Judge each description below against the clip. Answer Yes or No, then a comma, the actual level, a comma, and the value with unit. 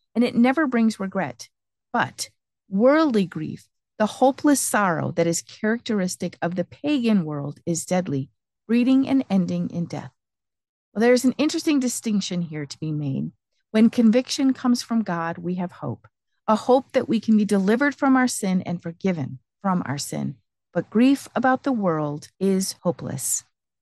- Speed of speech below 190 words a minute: Yes, average, 160 wpm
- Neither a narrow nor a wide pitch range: No, wide, 7.0 semitones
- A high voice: Yes, high, 195 Hz